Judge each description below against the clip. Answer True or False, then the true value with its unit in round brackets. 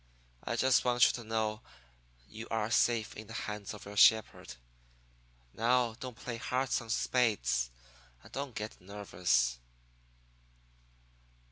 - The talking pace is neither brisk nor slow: False (130 wpm)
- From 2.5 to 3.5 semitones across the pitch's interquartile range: True (2.8 semitones)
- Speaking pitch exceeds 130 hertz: False (110 Hz)